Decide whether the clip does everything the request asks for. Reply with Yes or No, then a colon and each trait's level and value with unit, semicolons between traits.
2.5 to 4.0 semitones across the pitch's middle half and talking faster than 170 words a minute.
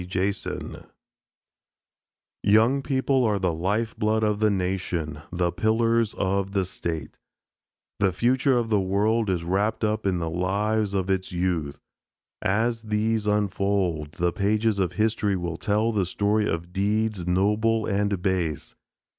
No: average, 3.1 semitones; average, 140 wpm